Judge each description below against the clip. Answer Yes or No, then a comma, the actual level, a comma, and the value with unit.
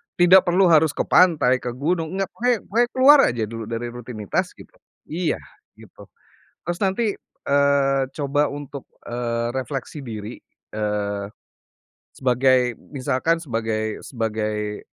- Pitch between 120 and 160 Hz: Yes, low, 135 Hz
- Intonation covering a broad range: Yes, wide, 6.4 semitones